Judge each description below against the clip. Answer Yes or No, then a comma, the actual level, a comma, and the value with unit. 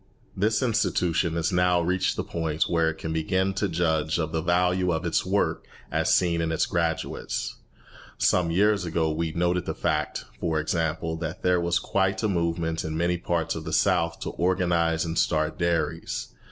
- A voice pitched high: No, very low, 85 Hz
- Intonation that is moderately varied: No, narrow, 1.8 semitones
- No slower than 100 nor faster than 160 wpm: No, average, 180 wpm